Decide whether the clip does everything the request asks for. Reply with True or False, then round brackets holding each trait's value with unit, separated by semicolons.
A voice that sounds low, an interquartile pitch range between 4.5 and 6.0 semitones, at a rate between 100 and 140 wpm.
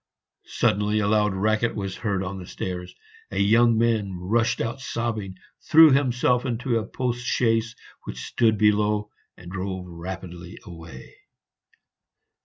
False (105 Hz; 3.9 semitones; 135 wpm)